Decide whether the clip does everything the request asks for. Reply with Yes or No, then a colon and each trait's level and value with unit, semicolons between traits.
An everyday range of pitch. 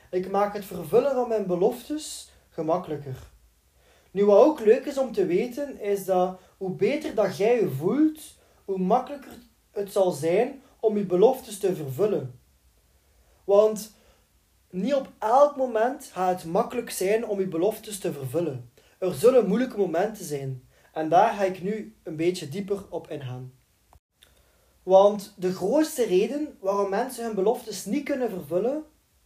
No: wide, 6.2 semitones